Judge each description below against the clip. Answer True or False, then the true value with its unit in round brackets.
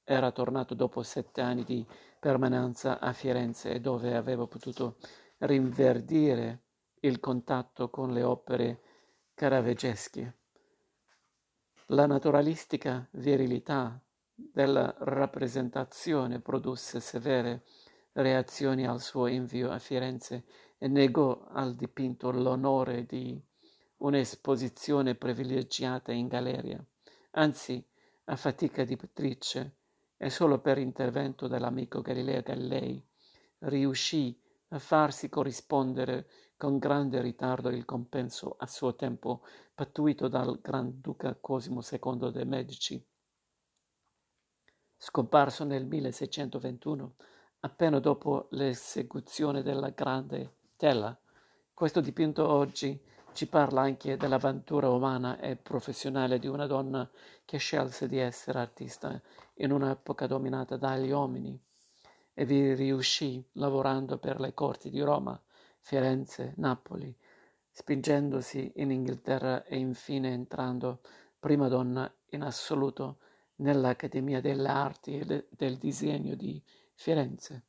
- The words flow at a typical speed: False (105 wpm)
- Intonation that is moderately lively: False (1.8 semitones)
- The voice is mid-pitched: False (130 Hz)